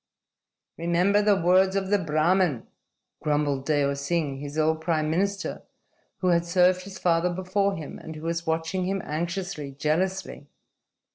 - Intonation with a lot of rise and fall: No, average, 3.5 semitones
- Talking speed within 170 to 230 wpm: No, average, 145 wpm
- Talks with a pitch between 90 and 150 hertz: No, medium, 170 Hz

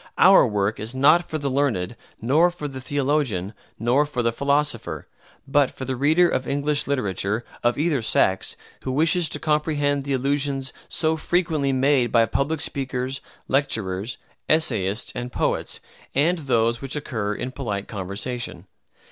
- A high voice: No, low, 135 Hz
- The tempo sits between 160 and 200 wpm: No, average, 150 wpm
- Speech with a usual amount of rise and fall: Yes, average, 4.0 semitones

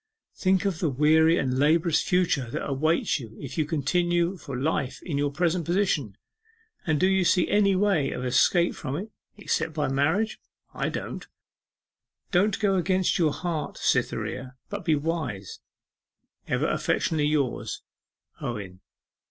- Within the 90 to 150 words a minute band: Yes, average, 145 wpm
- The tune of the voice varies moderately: Yes, average, 4.4 semitones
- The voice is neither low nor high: Yes, medium, 160 Hz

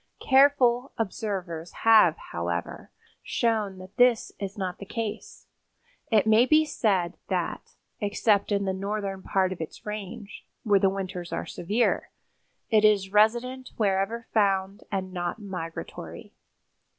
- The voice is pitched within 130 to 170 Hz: No, high, 200 Hz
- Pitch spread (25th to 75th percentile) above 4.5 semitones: No, average, 2.9 semitones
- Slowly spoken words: Yes, slow, 130 wpm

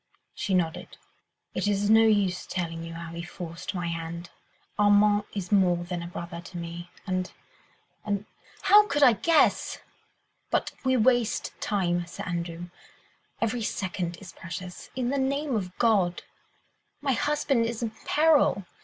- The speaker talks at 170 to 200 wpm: No, average, 150 wpm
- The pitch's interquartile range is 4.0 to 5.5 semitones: Yes, average, 4.8 semitones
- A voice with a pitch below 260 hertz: Yes, high, 190 Hz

